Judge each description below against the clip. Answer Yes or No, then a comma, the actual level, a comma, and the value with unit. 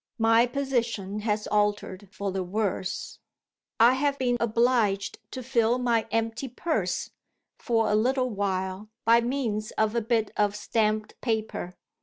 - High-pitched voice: Yes, high, 225 Hz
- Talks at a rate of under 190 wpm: Yes, average, 140 wpm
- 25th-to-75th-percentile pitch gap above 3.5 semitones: No, narrow, 2.5 semitones